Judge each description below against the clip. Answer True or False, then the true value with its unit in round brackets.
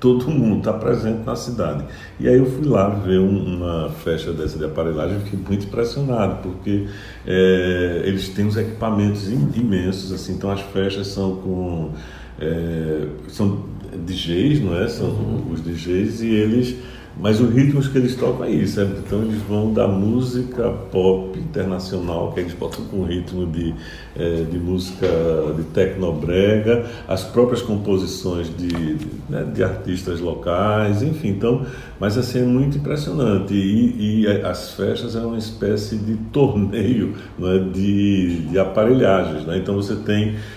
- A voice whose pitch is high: False (100 Hz)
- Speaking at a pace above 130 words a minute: True (160 wpm)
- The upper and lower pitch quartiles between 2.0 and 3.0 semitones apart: False (3.5 semitones)